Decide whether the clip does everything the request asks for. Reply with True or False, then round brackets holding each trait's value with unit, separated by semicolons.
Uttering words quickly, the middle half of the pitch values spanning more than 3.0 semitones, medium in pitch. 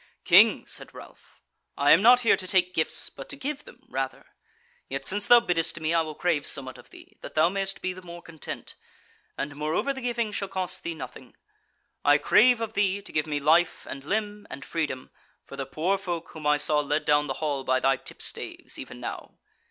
True (210 wpm; 5.2 semitones; 170 Hz)